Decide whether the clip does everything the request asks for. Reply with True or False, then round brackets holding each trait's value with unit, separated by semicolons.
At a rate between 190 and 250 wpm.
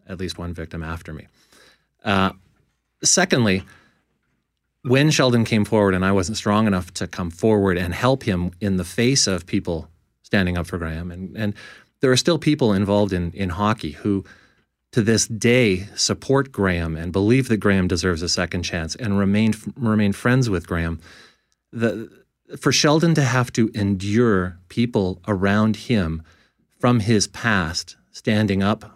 False (160 wpm)